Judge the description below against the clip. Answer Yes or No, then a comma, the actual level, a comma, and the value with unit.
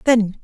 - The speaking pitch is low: No, high, 220 Hz